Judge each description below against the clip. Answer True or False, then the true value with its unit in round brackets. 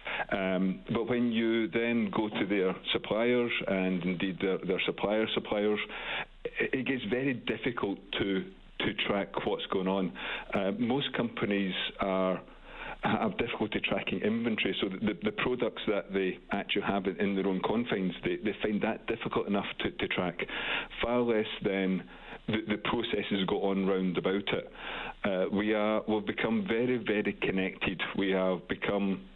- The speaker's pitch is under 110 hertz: True (100 Hz)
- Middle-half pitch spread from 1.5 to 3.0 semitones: True (2.6 semitones)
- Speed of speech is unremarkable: True (165 wpm)